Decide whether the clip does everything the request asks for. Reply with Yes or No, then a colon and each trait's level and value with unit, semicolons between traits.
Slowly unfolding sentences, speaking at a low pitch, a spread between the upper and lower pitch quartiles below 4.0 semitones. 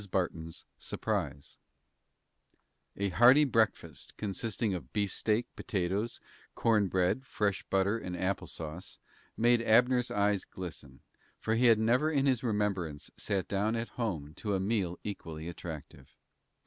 No: slow, 130 wpm; low, 100 Hz; average, 4.4 semitones